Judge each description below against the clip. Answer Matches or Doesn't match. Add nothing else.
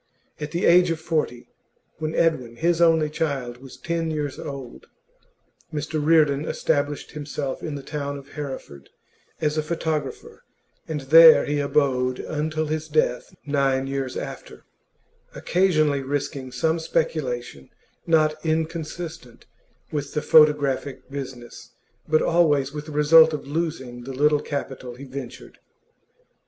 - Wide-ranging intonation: Doesn't match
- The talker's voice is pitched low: Doesn't match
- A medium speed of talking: Doesn't match